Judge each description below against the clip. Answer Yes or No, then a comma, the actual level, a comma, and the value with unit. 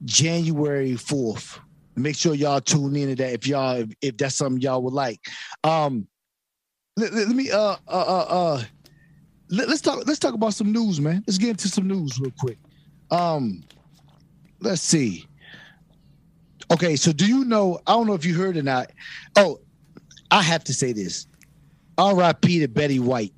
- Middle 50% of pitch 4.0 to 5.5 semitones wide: Yes, average, 4.5 semitones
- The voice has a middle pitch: Yes, medium, 160 Hz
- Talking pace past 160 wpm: Yes, average, 170 wpm